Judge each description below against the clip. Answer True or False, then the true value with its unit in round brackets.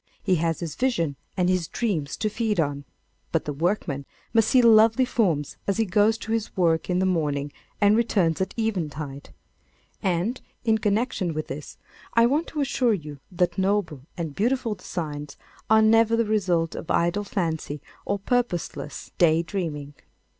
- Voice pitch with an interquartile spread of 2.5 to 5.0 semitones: False (5.6 semitones)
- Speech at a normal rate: True (165 wpm)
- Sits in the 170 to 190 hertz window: True (185 Hz)